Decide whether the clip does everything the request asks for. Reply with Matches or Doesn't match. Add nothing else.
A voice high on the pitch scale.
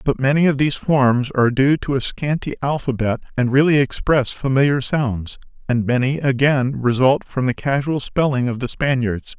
Doesn't match